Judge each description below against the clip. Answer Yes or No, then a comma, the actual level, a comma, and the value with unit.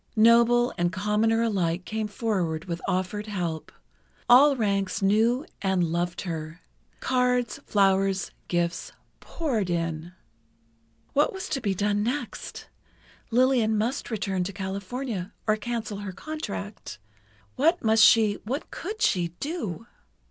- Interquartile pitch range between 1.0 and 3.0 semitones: No, average, 4.5 semitones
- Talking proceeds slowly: Yes, slow, 115 wpm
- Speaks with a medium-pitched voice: No, high, 210 Hz